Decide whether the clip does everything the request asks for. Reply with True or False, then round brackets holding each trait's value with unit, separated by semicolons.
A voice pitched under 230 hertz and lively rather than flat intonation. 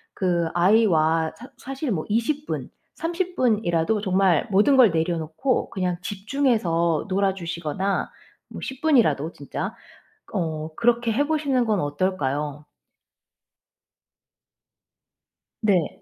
True (190 Hz; 6.7 semitones)